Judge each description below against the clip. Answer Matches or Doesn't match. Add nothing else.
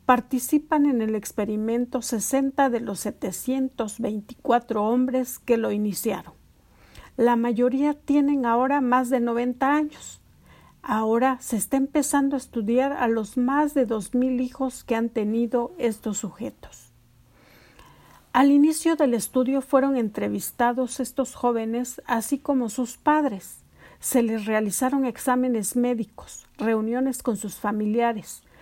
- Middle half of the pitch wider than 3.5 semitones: Doesn't match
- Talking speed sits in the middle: Doesn't match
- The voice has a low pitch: Doesn't match